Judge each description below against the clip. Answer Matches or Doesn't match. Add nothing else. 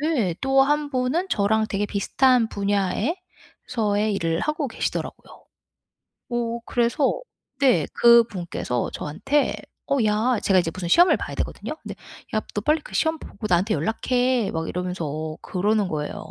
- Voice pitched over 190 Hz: Matches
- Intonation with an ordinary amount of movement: Doesn't match